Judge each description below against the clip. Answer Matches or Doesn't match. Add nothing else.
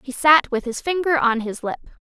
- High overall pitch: Matches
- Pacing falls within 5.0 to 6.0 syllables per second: Matches